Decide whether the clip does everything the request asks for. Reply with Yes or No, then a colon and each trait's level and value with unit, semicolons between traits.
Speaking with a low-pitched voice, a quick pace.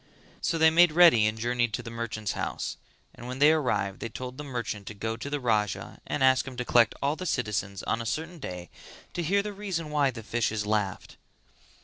Yes: low, 125 Hz; fast, 220 wpm